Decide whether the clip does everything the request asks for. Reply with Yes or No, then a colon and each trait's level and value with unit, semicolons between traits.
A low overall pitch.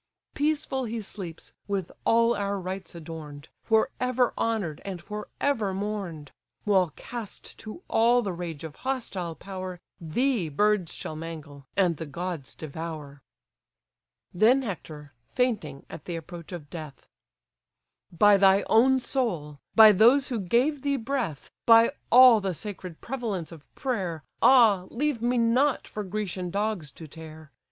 No: high, 195 Hz